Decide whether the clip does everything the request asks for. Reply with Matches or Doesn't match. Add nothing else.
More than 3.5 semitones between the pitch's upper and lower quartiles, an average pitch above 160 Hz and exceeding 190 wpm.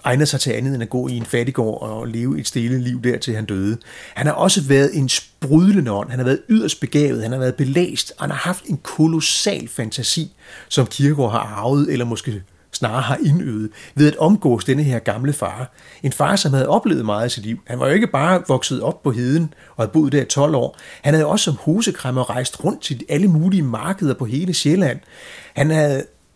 Doesn't match